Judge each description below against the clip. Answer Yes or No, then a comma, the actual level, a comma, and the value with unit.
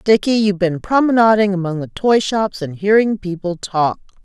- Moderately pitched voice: No, high, 195 Hz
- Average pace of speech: Yes, average, 170 wpm